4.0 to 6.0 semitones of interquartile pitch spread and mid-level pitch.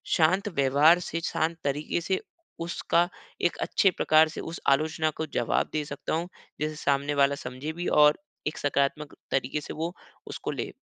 No: average, 2.8 semitones; medium, 155 Hz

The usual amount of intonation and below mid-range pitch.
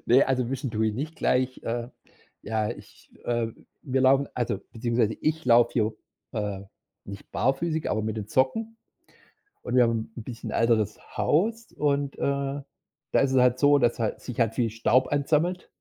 Yes: average, 3.6 semitones; low, 125 Hz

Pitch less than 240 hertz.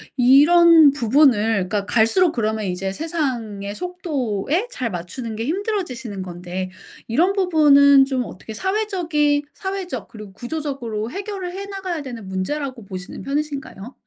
No: very high, 270 Hz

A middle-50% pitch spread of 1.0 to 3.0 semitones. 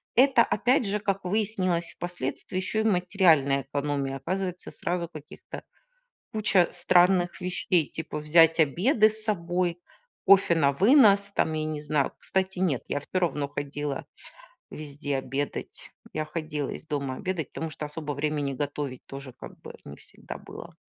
No: average, 4.6 semitones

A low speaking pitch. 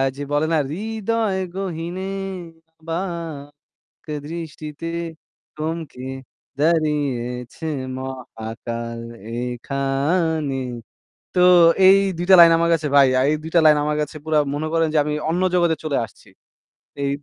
No: medium, 155 Hz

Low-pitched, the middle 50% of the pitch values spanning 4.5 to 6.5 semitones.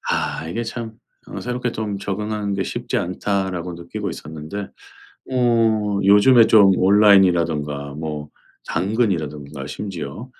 Yes: low, 100 Hz; average, 5.1 semitones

